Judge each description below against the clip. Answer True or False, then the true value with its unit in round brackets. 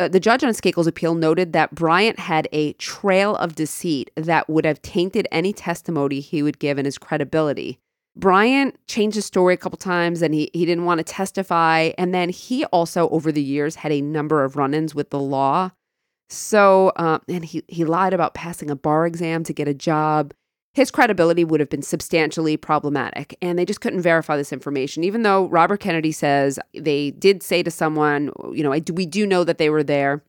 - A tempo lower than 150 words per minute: False (205 wpm)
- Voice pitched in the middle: True (165 Hz)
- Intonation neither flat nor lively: True (3.3 semitones)